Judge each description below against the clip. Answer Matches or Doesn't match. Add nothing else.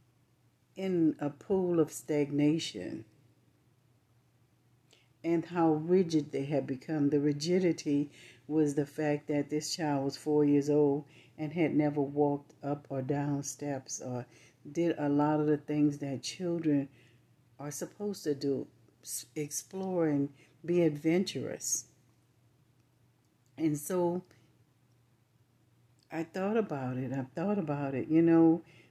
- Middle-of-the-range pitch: Matches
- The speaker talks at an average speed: Doesn't match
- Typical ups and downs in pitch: Matches